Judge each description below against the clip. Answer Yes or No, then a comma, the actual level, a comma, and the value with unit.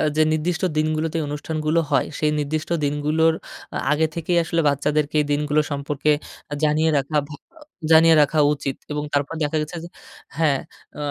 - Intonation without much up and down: Yes, narrow, 1.5 semitones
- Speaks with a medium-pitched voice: Yes, medium, 150 Hz